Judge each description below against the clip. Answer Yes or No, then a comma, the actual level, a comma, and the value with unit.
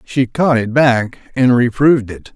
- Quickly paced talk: No, average, 180 wpm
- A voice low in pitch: Yes, low, 125 Hz